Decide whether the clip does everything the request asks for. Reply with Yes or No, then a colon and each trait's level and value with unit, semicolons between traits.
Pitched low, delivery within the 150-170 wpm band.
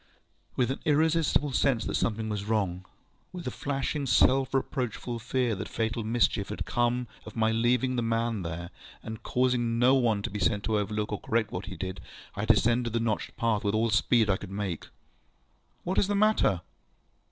No: low, 115 Hz; average, 185 wpm